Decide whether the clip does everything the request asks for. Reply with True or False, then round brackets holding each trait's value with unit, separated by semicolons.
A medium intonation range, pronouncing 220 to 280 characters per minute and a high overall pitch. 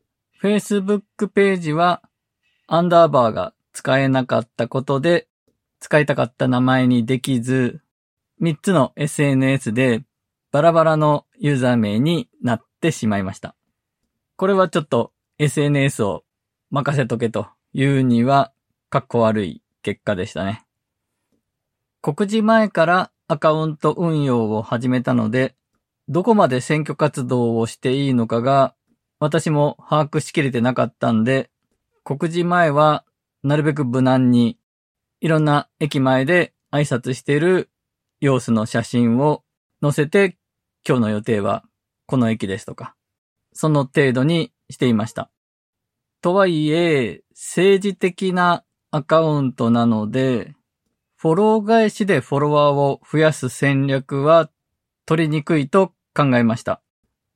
False (4.8 semitones; 260 characters per minute; 140 Hz)